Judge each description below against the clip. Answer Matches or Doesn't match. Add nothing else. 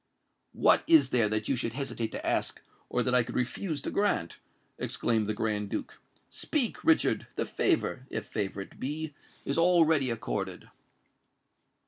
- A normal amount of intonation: Doesn't match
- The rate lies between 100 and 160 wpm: Matches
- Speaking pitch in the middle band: Doesn't match